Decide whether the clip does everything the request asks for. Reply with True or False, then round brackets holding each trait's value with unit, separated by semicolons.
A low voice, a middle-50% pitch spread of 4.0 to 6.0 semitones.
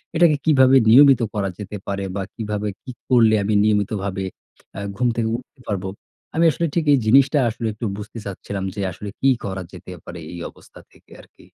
True (110 Hz; 4.7 semitones)